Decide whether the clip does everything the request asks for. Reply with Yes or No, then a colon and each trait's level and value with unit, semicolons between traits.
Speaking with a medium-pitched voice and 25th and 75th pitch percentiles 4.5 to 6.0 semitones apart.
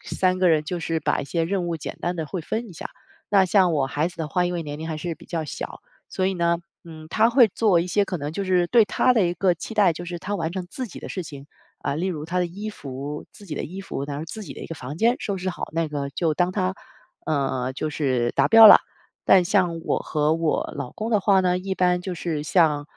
No: medium, 175 Hz; average, 3.5 semitones